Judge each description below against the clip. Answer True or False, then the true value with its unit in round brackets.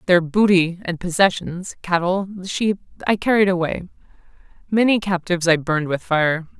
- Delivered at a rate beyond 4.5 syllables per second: True (5.0 syllables/s)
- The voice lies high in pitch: False (180 Hz)